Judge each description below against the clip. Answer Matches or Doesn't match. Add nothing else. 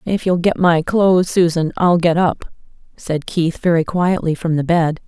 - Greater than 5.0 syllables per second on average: Doesn't match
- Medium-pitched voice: Matches